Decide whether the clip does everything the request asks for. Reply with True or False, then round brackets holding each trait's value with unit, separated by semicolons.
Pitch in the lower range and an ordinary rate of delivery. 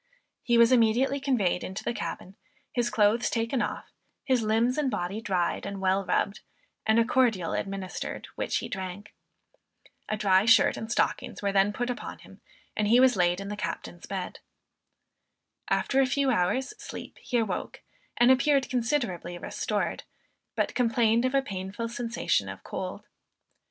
False (225 Hz; 160 wpm)